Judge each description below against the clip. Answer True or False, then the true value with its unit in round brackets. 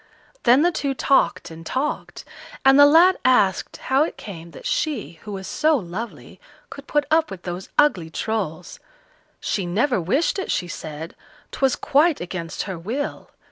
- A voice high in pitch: True (235 Hz)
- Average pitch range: False (8.6 semitones)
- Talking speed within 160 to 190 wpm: True (165 wpm)